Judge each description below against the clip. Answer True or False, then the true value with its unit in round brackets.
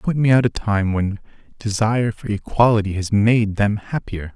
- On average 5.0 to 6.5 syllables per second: False (4.8 syllables/s)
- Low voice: True (105 Hz)